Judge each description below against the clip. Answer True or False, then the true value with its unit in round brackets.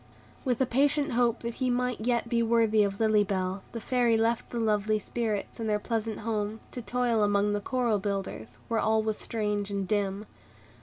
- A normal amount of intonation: False (2.3 semitones)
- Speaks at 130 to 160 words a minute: False (195 wpm)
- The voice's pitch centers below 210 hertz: False (220 Hz)